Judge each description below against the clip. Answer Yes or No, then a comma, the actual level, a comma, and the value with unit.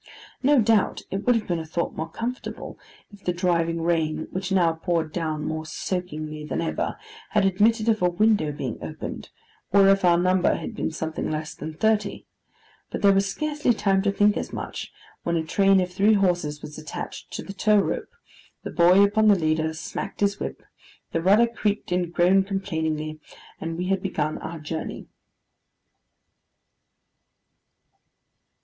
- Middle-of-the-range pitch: Yes, medium, 180 Hz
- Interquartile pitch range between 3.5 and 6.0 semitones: Yes, average, 4.0 semitones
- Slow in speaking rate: No, average, 170 wpm